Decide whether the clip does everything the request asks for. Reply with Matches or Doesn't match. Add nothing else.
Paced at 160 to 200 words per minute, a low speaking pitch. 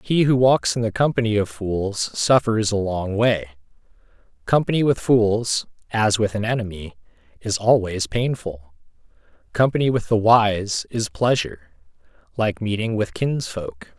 Doesn't match